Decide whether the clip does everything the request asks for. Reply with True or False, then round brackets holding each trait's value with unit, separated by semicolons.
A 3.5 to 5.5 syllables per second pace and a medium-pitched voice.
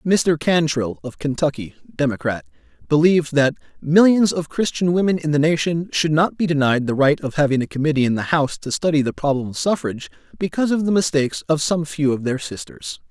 False (5.7 syllables/s; 155 Hz)